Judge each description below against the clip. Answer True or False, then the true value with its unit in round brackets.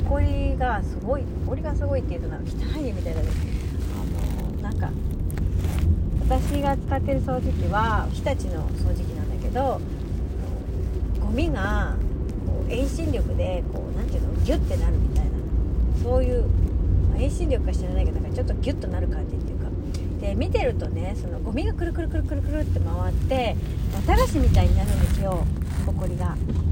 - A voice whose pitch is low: True (85 Hz)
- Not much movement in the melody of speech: True (1.9 semitones)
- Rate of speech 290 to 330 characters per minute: True (315 characters per minute)